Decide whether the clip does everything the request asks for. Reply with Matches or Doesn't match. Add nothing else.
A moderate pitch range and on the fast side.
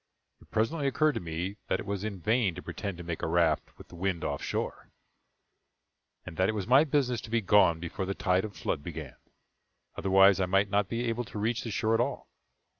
Matches